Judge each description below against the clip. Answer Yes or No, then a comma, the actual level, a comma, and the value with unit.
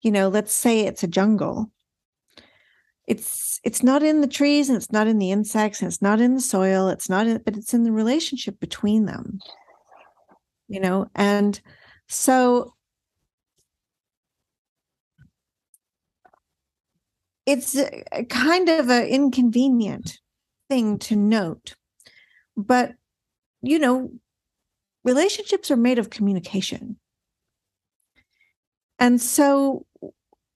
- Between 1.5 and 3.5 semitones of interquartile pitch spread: No, average, 4.0 semitones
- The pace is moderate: No, slow, 110 wpm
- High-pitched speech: Yes, high, 235 Hz